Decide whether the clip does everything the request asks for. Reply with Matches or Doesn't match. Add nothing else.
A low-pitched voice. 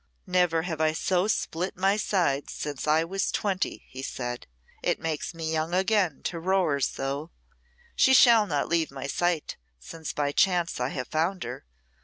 Doesn't match